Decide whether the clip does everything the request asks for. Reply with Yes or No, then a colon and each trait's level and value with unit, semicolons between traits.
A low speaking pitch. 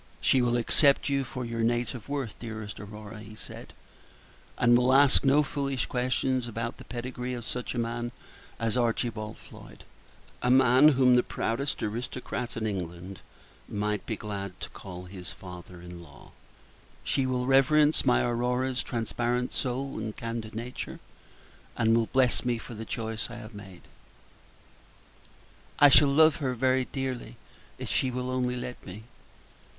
Yes: low, 120 Hz